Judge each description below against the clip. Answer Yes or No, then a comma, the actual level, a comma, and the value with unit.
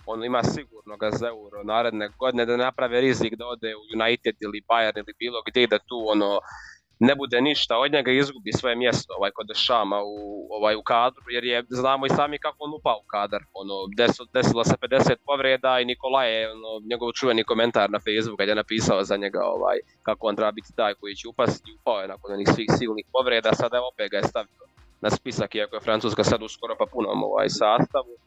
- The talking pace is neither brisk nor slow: No, fast, 215 wpm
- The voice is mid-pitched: No, low, 115 Hz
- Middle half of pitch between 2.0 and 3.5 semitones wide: Yes, average, 3.0 semitones